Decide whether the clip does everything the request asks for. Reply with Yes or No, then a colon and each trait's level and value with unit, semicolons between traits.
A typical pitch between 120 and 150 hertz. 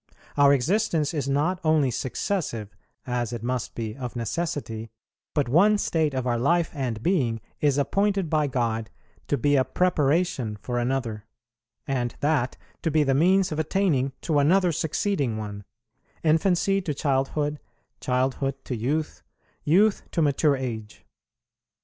Yes: medium, 140 Hz